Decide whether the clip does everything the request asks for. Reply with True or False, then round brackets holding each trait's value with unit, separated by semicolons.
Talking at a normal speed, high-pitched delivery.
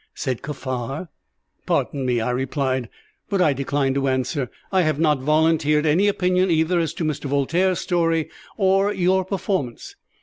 False (155 wpm; 155 Hz)